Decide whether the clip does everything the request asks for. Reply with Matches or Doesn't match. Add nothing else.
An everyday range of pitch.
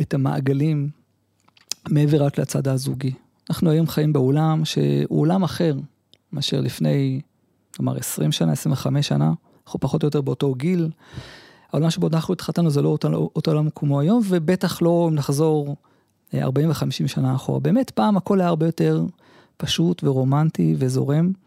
Matches